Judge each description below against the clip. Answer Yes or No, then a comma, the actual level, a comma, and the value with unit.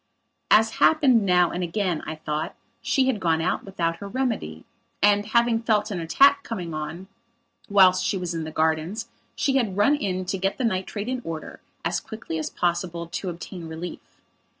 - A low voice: No, medium, 185 Hz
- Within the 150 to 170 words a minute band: No, average, 180 wpm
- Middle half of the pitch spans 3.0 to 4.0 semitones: No, average, 4.9 semitones